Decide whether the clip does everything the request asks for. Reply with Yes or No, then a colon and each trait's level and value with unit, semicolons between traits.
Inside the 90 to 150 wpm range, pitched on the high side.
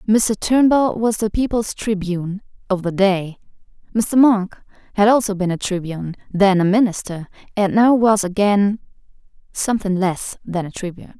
Yes: average, 145 wpm; high, 200 Hz